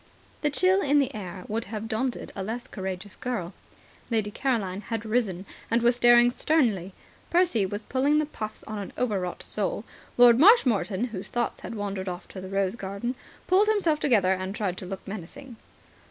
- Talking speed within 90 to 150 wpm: No, average, 180 wpm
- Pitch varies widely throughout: No, average, 4.5 semitones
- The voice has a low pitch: No, high, 220 Hz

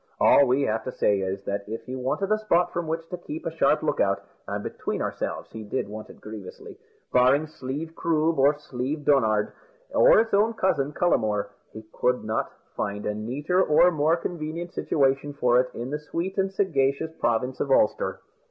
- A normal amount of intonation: No, wide, 5.7 semitones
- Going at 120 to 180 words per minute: No, average, 190 wpm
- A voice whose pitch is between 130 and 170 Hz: Yes, medium, 140 Hz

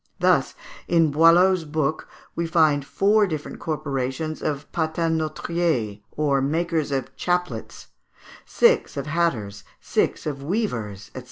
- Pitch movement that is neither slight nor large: Yes, average, 3.6 semitones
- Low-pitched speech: No, medium, 155 Hz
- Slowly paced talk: Yes, slow, 115 wpm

